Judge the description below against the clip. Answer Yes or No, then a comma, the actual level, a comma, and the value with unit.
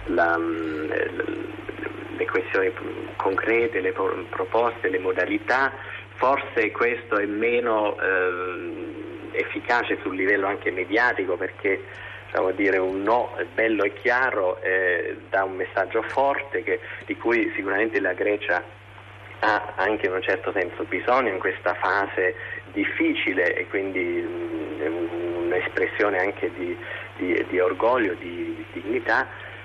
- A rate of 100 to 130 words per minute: Yes, average, 120 wpm